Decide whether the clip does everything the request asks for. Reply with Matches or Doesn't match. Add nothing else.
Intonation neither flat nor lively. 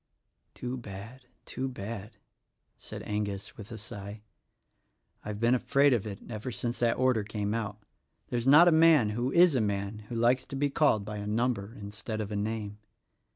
Matches